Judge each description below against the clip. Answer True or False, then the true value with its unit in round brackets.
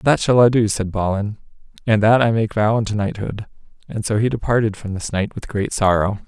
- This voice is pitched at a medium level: False (105 Hz)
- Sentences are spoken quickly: True (220 wpm)